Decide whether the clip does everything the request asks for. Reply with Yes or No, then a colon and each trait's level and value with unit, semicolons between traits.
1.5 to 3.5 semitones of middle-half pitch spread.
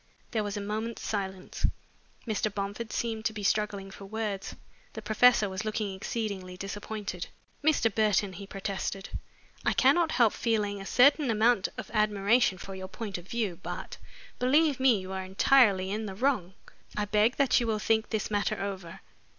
Yes: narrow, 2.6 semitones